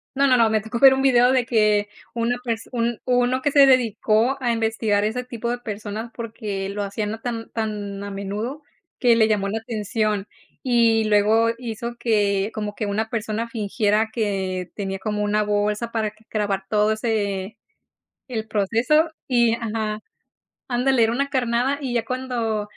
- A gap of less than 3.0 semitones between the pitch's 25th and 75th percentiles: Yes, narrow, 2.4 semitones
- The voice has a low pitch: No, high, 225 Hz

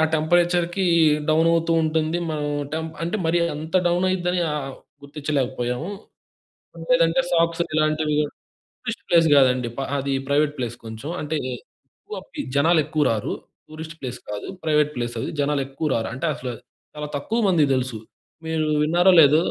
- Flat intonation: No, average, 3.3 semitones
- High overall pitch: No, medium, 155 Hz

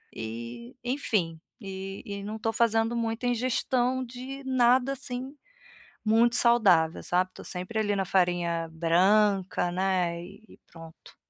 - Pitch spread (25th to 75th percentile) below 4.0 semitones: No, average, 5.2 semitones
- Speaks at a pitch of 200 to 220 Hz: Yes, high, 210 Hz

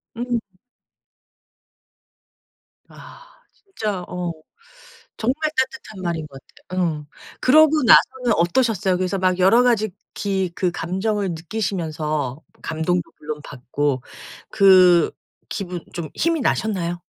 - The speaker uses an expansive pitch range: No, average, 4.9 semitones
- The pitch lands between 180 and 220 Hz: Yes, medium, 185 Hz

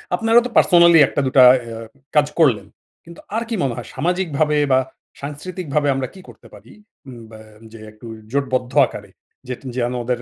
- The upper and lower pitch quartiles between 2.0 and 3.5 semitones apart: No, average, 5.3 semitones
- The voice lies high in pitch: No, medium, 140 Hz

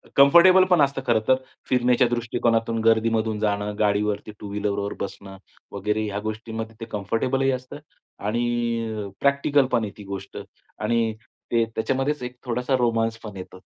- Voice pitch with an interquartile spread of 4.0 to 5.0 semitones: No, average, 3.0 semitones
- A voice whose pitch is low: Yes, low, 115 Hz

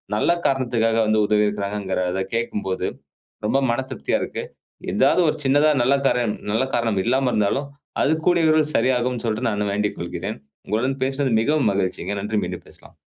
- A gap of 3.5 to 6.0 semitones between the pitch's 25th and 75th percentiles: Yes, average, 4.4 semitones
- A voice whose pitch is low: Yes, low, 115 Hz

